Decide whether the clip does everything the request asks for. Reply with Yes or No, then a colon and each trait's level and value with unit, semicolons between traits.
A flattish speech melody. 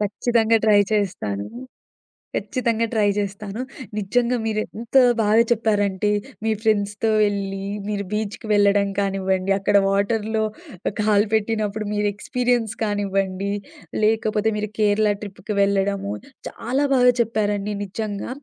Yes: narrow, 1.8 semitones